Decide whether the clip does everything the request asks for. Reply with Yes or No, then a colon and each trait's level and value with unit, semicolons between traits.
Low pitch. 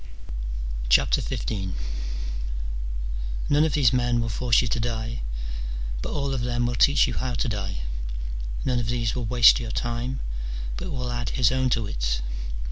Yes: low, 120 Hz